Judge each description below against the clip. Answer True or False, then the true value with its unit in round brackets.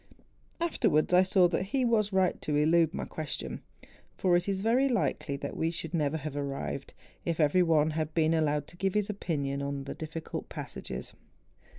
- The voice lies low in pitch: False (165 Hz)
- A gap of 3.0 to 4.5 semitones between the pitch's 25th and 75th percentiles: True (4.2 semitones)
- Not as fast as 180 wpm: False (185 wpm)